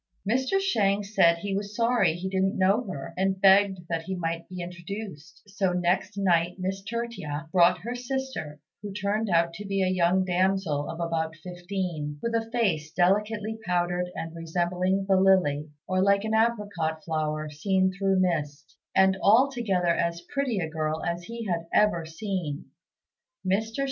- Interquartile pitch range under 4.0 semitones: Yes, average, 3.2 semitones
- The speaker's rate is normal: Yes, average, 165 wpm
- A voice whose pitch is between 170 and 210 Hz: Yes, medium, 185 Hz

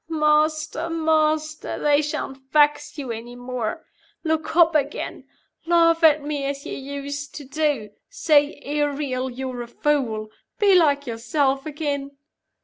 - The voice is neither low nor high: No, very high, 290 Hz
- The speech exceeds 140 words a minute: No, slow, 135 wpm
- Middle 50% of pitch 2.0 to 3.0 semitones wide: Yes, narrow, 2.5 semitones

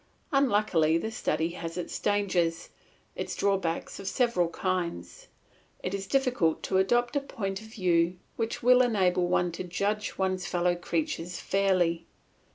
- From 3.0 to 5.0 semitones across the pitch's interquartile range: Yes, average, 3.8 semitones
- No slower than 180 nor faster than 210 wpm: No, average, 145 wpm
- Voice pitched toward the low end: No, medium, 185 Hz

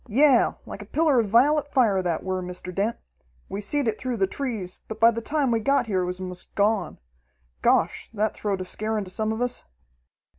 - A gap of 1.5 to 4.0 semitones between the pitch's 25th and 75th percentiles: No, average, 4.4 semitones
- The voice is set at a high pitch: Yes, high, 220 Hz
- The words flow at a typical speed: No, fast, 215 wpm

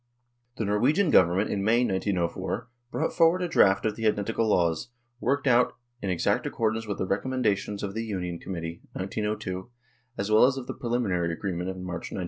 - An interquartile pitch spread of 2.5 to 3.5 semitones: No, average, 4.2 semitones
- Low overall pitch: Yes, low, 105 Hz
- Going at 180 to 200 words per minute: Yes, average, 185 wpm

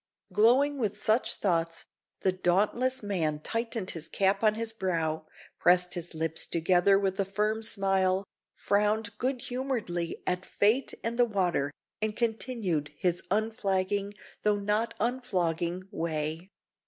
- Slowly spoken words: Yes, slow, 130 wpm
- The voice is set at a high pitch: Yes, high, 195 Hz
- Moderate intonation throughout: Yes, average, 3.9 semitones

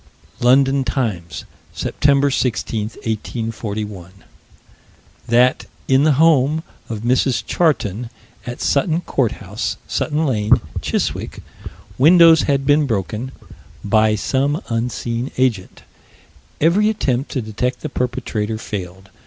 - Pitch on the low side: Yes, low, 125 Hz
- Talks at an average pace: No, slow, 105 wpm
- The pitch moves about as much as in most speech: Yes, average, 4.3 semitones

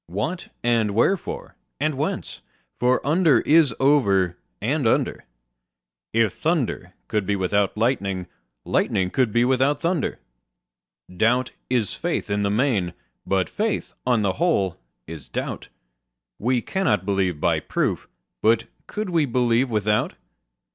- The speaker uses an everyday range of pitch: No, wide, 5.8 semitones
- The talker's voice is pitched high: No, low, 115 Hz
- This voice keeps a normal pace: No, slow, 130 wpm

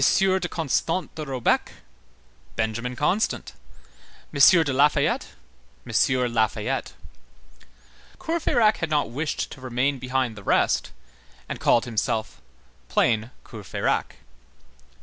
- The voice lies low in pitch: Yes, low, 130 Hz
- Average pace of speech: No, slow, 100 wpm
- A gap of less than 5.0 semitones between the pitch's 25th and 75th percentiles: No, average, 5.3 semitones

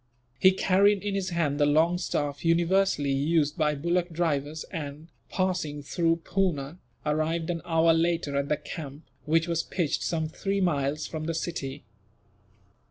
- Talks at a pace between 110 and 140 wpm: No, average, 155 wpm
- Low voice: No, medium, 165 Hz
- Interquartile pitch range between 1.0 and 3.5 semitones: Yes, average, 2.8 semitones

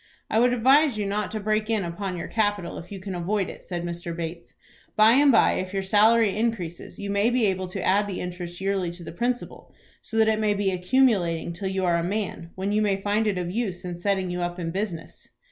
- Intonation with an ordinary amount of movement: Yes, average, 3.4 semitones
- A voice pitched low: No, high, 195 Hz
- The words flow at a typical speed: No, fast, 240 wpm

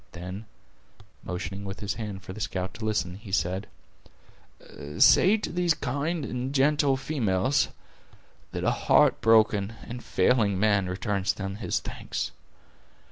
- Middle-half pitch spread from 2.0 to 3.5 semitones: No, average, 5.2 semitones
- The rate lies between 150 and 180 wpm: No, slow, 135 wpm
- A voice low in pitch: Yes, low, 105 Hz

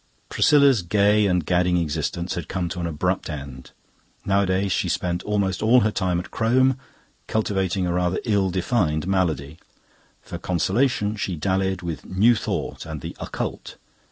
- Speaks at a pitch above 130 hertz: No, very low, 95 Hz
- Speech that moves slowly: No, average, 155 wpm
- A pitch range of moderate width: Yes, average, 3.1 semitones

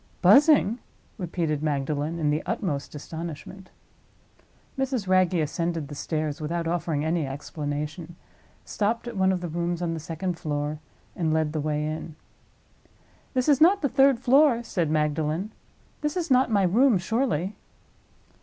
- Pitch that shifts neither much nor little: No, wide, 5.9 semitones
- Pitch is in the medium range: Yes, medium, 170 Hz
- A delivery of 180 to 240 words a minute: No, average, 145 wpm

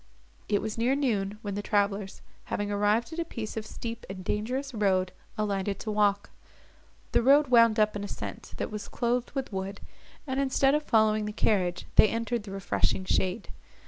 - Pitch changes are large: No, average, 2.8 semitones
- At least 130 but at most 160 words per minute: No, average, 180 wpm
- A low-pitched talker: No, high, 215 Hz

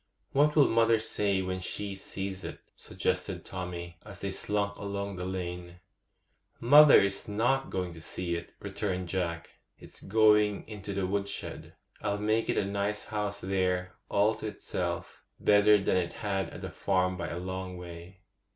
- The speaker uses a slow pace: No, average, 165 wpm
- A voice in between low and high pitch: No, low, 100 Hz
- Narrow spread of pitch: Yes, narrow, 2.3 semitones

